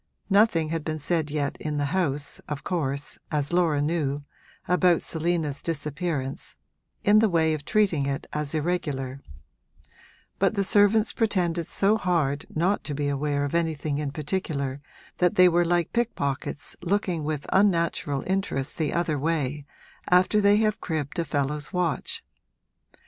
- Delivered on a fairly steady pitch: No, average, 3.8 semitones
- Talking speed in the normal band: Yes, average, 150 wpm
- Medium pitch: Yes, medium, 160 Hz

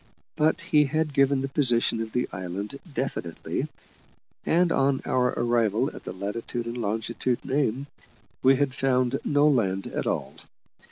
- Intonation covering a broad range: No, average, 3.6 semitones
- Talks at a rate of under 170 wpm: Yes, average, 150 wpm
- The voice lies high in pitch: No, low, 130 Hz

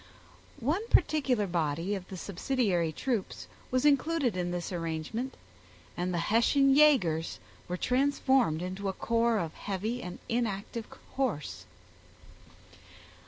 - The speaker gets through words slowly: Yes, slow, 120 wpm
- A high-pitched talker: Yes, high, 210 Hz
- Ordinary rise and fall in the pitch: No, wide, 6.6 semitones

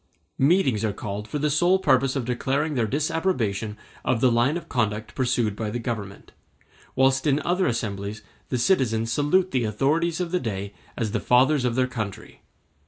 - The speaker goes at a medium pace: Yes, average, 175 wpm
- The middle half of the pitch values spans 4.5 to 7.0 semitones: Yes, average, 5.2 semitones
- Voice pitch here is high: No, low, 125 Hz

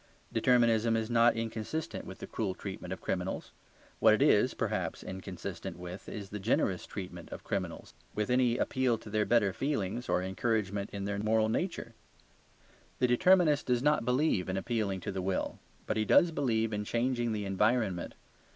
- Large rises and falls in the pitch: No, average, 3.8 semitones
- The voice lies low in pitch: Yes, low, 110 Hz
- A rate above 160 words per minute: Yes, average, 170 wpm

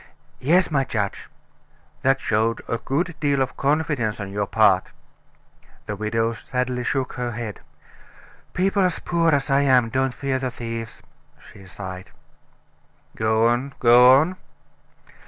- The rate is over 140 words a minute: No, slow, 135 wpm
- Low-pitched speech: Yes, low, 125 Hz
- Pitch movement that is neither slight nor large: Yes, average, 3.6 semitones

